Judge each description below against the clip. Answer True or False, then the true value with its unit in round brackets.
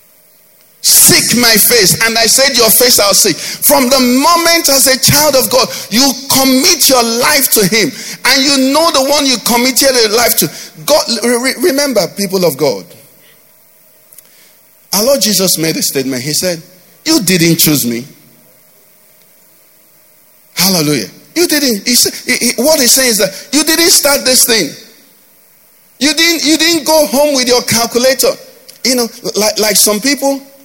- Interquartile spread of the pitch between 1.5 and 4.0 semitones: False (5.1 semitones)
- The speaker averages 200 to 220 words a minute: False (160 wpm)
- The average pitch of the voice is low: False (250 Hz)